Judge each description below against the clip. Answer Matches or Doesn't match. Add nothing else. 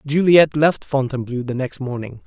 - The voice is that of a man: Matches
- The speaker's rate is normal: Matches